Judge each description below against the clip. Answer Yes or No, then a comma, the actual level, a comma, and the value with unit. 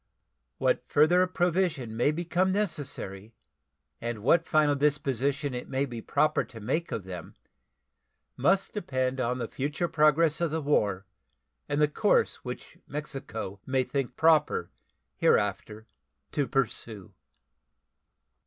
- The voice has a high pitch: No, medium, 140 Hz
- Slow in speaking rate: Yes, slow, 125 wpm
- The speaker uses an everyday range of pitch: Yes, average, 4.9 semitones